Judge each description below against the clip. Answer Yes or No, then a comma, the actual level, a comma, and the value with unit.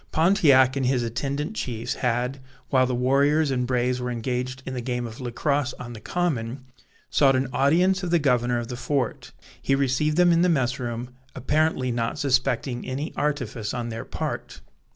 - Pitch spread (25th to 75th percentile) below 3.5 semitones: Yes, average, 2.8 semitones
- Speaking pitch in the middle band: No, low, 130 Hz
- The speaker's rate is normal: Yes, average, 180 wpm